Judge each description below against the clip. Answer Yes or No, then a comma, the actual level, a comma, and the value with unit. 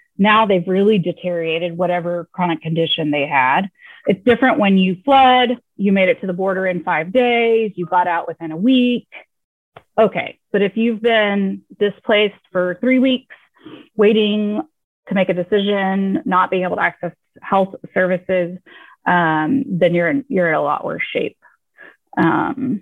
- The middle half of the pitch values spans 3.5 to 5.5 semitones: Yes, average, 4.5 semitones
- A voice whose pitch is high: Yes, high, 195 Hz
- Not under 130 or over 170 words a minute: Yes, average, 160 wpm